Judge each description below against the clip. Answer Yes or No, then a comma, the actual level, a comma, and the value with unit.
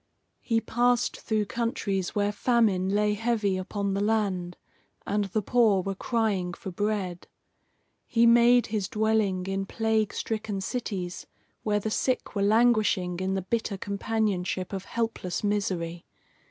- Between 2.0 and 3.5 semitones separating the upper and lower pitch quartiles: Yes, average, 2.7 semitones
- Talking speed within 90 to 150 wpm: Yes, average, 140 wpm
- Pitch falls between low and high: No, high, 205 Hz